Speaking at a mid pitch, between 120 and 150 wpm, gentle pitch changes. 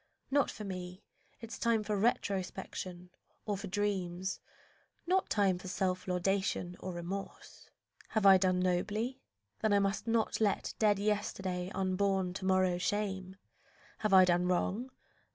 No: high, 195 Hz; average, 140 wpm; narrow, 2.2 semitones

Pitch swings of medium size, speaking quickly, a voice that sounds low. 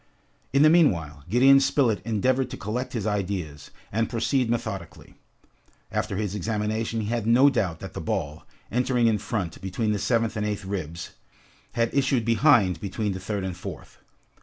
No: average, 4.0 semitones; average, 165 wpm; low, 110 Hz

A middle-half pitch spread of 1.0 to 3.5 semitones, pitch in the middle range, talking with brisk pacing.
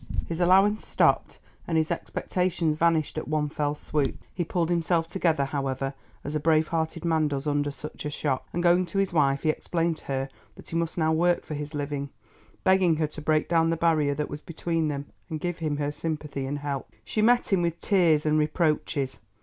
Yes: narrow, 2.6 semitones; medium, 155 Hz; fast, 210 wpm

